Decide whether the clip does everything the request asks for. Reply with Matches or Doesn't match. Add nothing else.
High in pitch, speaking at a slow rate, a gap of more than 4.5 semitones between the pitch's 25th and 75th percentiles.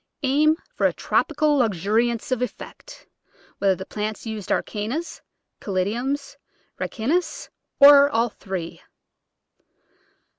Matches